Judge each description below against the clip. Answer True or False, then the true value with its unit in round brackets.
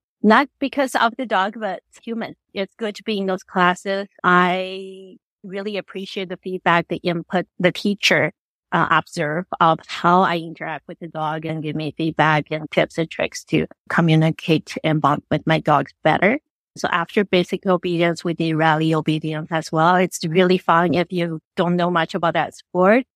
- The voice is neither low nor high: True (175 Hz)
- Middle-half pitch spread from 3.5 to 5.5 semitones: False (3.1 semitones)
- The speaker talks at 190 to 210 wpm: False (180 wpm)